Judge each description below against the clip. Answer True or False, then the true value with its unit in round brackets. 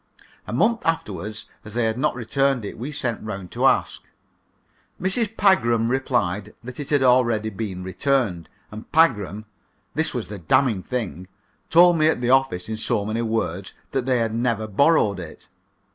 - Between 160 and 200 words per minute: True (170 wpm)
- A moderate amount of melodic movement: True (4.3 semitones)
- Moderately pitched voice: False (115 Hz)